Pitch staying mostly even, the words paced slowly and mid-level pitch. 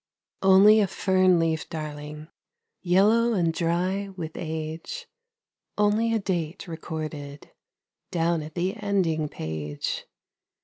No: average, 3.9 semitones; slow, 105 wpm; medium, 170 Hz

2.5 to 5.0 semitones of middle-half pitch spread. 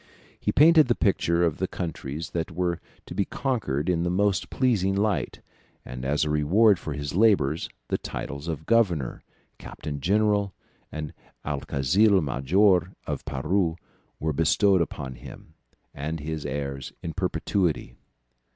No: wide, 5.4 semitones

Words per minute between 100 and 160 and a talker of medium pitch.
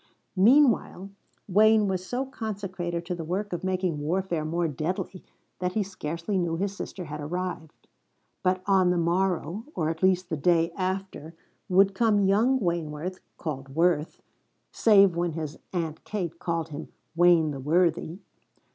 Yes: average, 150 wpm; medium, 180 Hz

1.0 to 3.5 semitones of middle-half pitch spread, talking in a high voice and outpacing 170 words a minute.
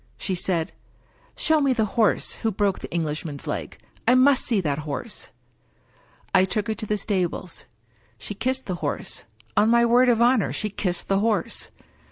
No: average, 4.6 semitones; high, 210 Hz; average, 185 wpm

